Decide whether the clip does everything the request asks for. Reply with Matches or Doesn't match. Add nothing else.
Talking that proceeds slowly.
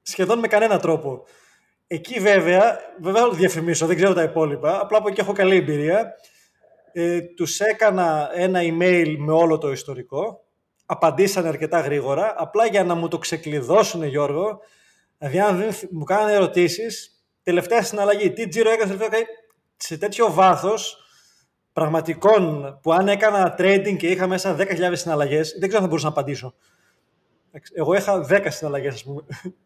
Doesn't match